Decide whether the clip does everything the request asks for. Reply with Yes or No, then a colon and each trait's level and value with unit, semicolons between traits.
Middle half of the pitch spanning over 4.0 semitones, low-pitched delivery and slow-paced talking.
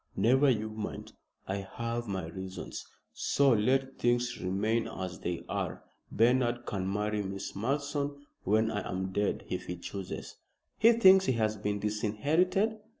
No: average, 5.0 semitones; low, 110 Hz; average, 150 wpm